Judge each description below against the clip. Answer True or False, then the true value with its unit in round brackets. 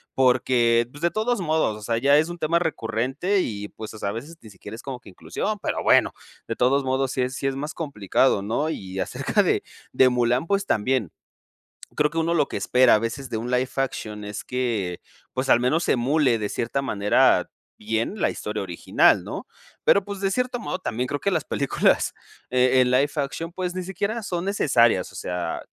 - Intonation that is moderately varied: False (6.0 semitones)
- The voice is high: False (130 Hz)